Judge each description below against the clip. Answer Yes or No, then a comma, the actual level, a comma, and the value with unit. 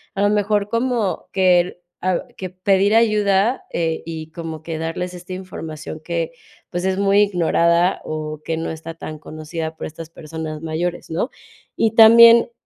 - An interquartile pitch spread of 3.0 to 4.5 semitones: Yes, average, 3.8 semitones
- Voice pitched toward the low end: No, medium, 175 Hz